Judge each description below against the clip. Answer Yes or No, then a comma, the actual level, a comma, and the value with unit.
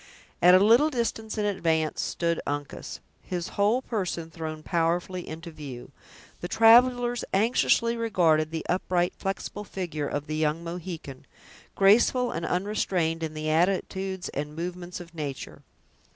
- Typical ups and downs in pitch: Yes, average, 4.3 semitones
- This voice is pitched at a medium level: Yes, medium, 175 Hz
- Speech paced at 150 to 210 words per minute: No, slow, 135 wpm